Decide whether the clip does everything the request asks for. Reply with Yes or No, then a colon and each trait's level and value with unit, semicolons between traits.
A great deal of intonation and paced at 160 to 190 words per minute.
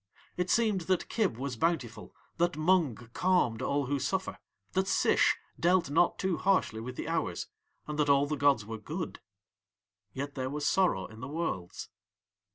Yes: wide, 5.8 semitones; average, 165 wpm